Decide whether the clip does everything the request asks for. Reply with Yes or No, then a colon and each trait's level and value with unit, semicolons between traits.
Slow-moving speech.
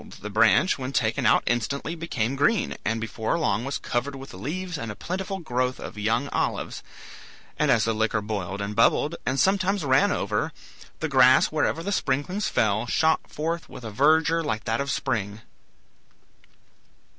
No: average, 170 wpm